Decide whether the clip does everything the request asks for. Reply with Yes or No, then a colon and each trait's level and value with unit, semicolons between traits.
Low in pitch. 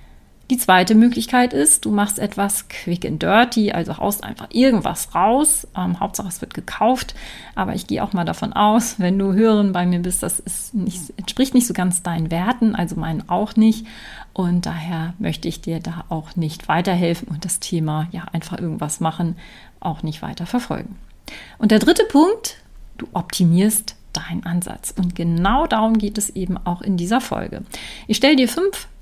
No: high, 190 Hz